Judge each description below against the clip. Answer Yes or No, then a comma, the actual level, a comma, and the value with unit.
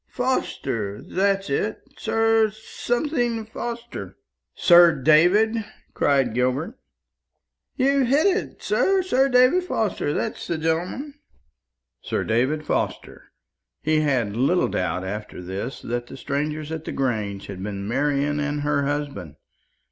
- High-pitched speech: No, medium, 155 Hz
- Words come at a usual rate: No, slow, 125 wpm